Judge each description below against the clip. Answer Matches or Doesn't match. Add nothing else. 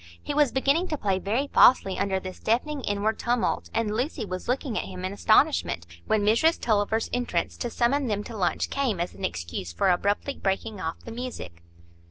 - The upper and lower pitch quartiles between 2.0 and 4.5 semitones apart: Doesn't match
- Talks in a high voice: Matches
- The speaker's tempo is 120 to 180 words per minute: Doesn't match